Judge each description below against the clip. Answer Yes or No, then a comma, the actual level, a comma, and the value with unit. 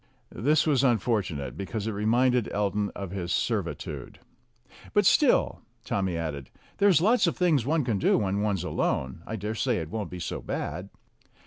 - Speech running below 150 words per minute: No, average, 165 wpm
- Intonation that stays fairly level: No, average, 5.2 semitones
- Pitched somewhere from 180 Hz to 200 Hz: No, low, 105 Hz